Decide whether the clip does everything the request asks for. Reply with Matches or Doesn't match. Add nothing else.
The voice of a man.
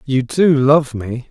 Matches